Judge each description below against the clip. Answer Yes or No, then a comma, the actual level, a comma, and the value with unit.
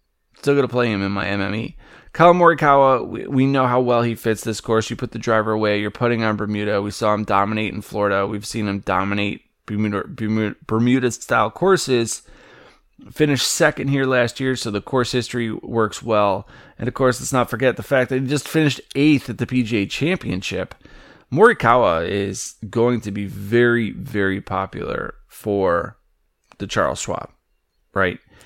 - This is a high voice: No, low, 115 Hz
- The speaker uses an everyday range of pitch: Yes, average, 3.9 semitones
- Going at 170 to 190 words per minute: Yes, average, 175 wpm